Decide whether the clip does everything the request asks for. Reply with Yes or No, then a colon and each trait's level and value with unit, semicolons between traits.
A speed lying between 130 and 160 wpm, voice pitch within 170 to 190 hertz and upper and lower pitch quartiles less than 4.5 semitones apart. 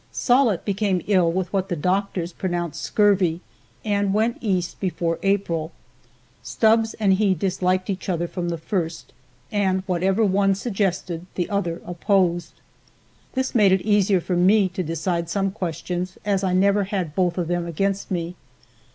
Yes: average, 155 wpm; medium, 185 Hz; narrow, 2.4 semitones